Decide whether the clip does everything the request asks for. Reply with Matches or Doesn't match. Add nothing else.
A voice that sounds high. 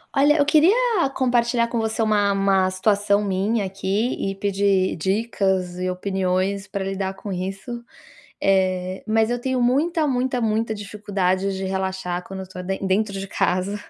Matches